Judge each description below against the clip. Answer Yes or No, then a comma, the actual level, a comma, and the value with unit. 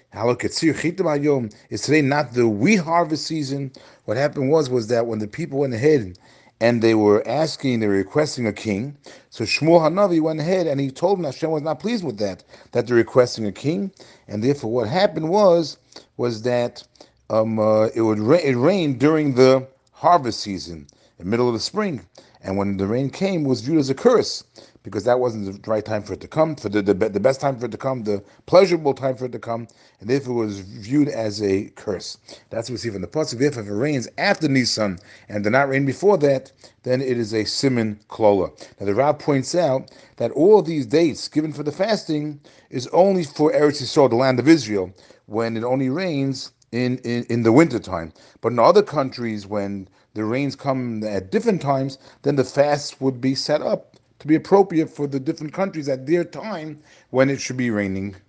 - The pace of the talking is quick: Yes, fast, 210 wpm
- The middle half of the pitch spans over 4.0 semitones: Yes, wide, 5.5 semitones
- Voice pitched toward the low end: Yes, low, 130 Hz